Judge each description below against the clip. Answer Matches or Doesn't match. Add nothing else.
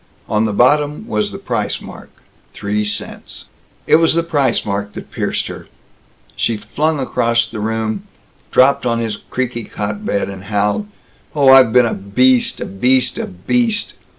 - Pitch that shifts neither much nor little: Matches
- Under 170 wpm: Matches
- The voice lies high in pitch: Doesn't match